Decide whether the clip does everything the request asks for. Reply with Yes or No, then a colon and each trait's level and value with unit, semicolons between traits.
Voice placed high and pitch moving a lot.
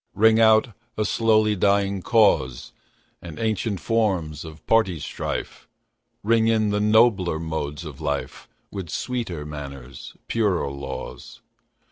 No: low, 100 Hz; wide, 6.0 semitones